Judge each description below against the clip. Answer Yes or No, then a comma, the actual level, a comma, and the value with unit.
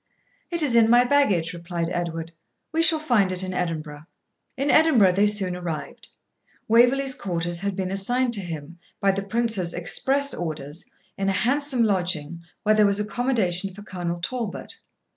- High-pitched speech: Yes, high, 195 Hz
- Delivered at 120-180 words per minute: Yes, average, 160 wpm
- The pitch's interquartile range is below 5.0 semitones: No, wide, 5.6 semitones